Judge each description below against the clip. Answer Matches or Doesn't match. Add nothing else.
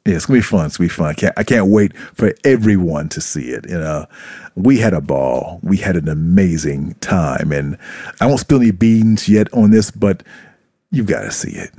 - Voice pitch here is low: Matches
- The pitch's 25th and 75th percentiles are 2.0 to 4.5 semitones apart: Doesn't match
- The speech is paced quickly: Matches